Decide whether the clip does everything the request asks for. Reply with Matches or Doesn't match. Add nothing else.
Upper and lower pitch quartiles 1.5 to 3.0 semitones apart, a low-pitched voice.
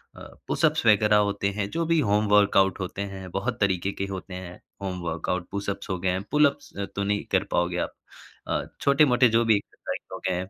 Matches